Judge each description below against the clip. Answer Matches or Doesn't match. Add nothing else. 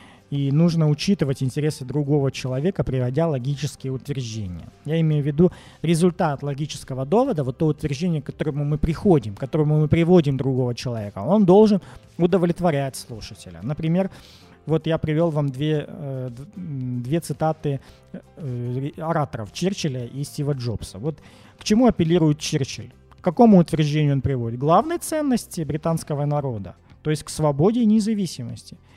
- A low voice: Doesn't match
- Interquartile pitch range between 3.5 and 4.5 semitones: Matches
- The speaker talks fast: Doesn't match